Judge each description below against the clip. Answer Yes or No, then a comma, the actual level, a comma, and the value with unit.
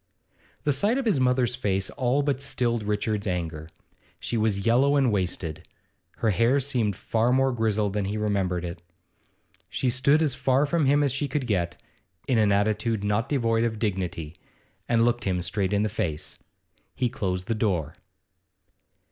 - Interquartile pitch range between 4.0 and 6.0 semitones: Yes, average, 4.7 semitones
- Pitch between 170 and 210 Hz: No, low, 110 Hz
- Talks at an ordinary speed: Yes, average, 170 wpm